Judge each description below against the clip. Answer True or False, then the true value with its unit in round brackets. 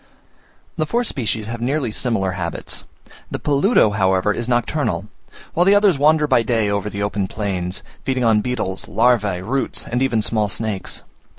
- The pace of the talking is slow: False (165 wpm)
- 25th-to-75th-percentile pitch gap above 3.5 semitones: True (4.6 semitones)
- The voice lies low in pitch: True (115 Hz)